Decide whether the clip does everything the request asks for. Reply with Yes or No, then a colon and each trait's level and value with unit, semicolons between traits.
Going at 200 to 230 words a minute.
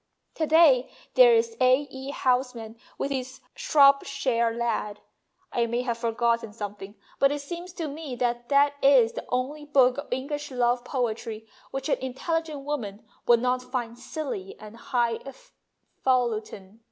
No: average, 150 wpm